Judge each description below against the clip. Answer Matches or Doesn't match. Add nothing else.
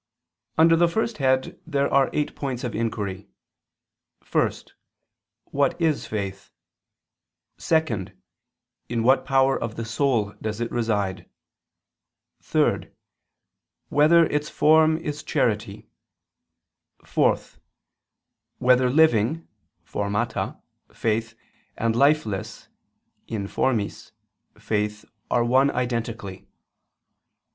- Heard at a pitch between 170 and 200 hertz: Doesn't match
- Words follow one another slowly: Matches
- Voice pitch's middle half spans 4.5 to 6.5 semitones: Matches